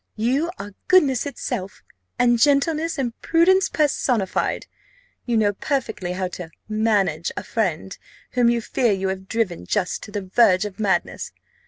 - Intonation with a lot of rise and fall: Yes, wide, 5.8 semitones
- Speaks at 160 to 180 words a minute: No, average, 150 wpm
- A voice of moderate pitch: No, high, 220 Hz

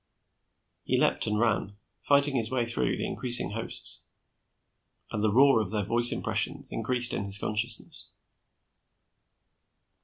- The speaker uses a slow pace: Yes, slow, 130 wpm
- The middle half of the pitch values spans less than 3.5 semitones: Yes, narrow, 2.4 semitones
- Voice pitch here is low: Yes, low, 115 Hz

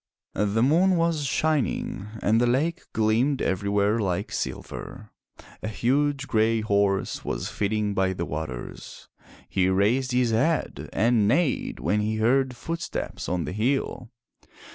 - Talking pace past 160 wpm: No, slow, 135 wpm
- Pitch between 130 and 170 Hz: No, low, 110 Hz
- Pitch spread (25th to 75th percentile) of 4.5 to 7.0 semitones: Yes, average, 5.0 semitones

